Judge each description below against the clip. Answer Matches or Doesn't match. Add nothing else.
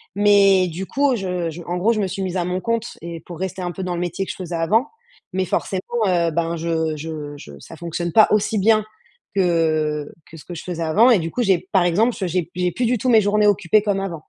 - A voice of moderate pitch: Matches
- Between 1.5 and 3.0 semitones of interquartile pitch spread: Doesn't match